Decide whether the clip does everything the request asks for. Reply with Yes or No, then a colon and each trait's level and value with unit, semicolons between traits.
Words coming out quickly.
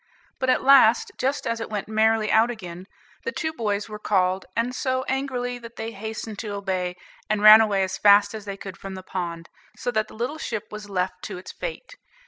Yes: fast, 215 wpm